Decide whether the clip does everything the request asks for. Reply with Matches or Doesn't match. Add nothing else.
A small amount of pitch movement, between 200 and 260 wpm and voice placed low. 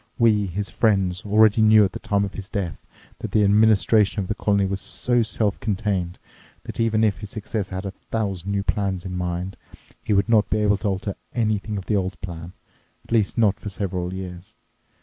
Matches